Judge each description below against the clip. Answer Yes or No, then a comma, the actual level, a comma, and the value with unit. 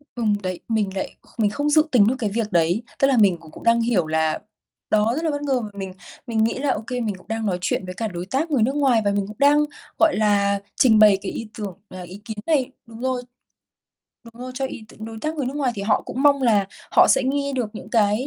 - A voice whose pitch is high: Yes, high, 225 Hz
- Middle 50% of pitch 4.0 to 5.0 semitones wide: Yes, average, 4.6 semitones